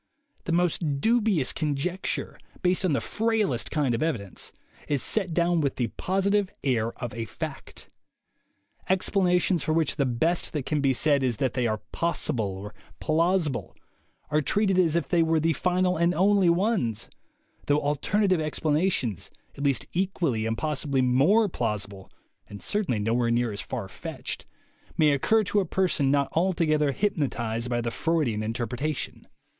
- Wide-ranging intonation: Yes, wide, 6.6 semitones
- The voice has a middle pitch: Yes, medium, 150 Hz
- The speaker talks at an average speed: Yes, average, 160 wpm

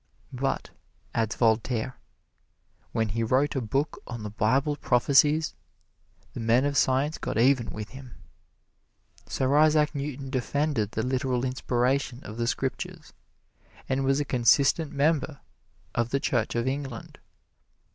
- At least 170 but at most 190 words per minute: No, slow, 135 wpm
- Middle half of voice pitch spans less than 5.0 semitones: Yes, average, 3.0 semitones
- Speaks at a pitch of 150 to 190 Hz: No, low, 130 Hz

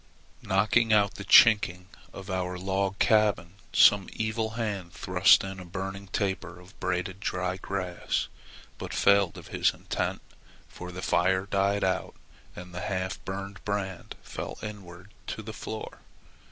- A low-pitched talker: Yes, very low, 95 Hz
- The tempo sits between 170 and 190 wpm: No, average, 145 wpm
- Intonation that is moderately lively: No, narrow, 1.9 semitones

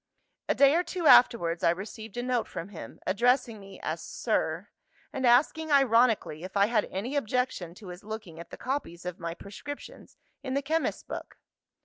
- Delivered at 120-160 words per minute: No, average, 180 wpm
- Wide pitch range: Yes, wide, 6.3 semitones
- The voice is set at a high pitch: Yes, high, 225 Hz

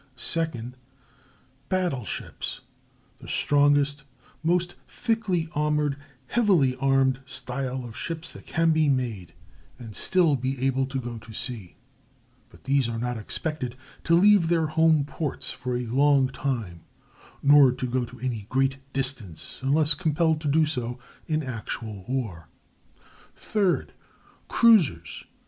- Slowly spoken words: Yes, slow, 130 wpm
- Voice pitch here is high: No, low, 135 Hz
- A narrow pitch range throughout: No, average, 4.3 semitones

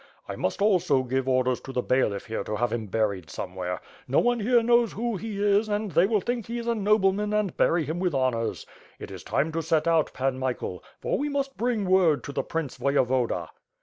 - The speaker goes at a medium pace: No, fast, 220 wpm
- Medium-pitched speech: Yes, medium, 165 Hz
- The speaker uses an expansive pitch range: Yes, wide, 8.7 semitones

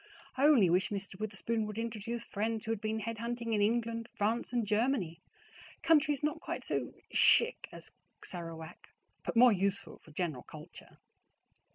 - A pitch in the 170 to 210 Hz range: No, high, 220 Hz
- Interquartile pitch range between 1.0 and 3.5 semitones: Yes, average, 2.9 semitones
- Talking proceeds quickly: No, average, 160 wpm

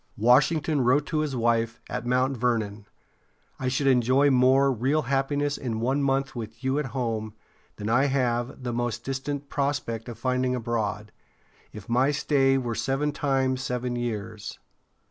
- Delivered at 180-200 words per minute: No, average, 155 wpm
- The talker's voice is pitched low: Yes, low, 130 Hz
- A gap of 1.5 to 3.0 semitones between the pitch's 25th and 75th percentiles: Yes, narrow, 2.6 semitones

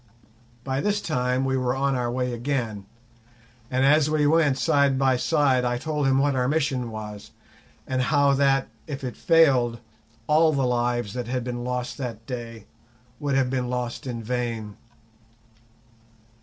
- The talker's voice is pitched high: No, low, 130 Hz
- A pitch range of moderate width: No, narrow, 2.3 semitones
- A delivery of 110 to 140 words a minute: No, average, 160 wpm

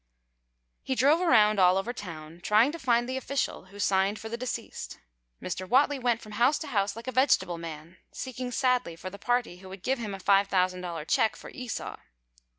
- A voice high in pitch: Yes, high, 215 Hz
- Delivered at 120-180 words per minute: No, average, 195 wpm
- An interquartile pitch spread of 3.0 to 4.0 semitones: No, average, 5.2 semitones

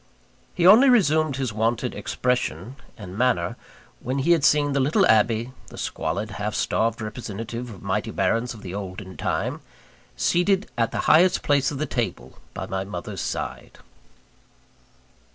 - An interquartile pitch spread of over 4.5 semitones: Yes, wide, 5.5 semitones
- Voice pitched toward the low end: Yes, low, 120 Hz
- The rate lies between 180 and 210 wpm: No, average, 155 wpm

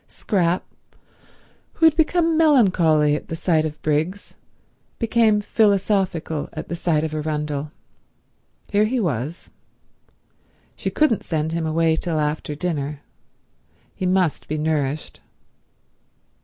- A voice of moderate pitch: Yes, medium, 165 Hz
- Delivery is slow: Yes, slow, 115 wpm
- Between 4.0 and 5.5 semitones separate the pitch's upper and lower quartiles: Yes, average, 5.0 semitones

